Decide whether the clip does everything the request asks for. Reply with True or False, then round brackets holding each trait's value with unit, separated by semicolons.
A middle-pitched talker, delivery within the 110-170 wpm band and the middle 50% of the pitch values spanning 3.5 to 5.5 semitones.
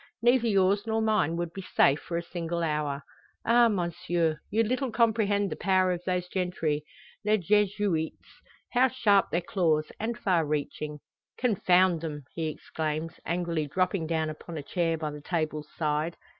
True (175 Hz; 160 wpm; 4.4 semitones)